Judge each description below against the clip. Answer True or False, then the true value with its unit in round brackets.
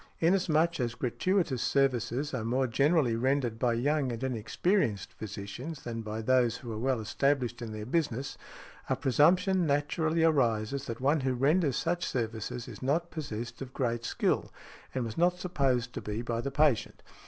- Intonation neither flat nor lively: True (4.5 semitones)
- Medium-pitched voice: False (130 Hz)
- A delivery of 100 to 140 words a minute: False (165 wpm)